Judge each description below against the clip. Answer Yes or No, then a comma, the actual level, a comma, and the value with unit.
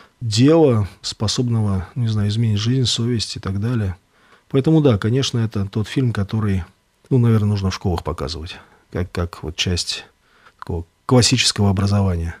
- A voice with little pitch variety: No, average, 3.9 semitones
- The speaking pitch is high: No, low, 105 Hz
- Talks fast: No, average, 145 wpm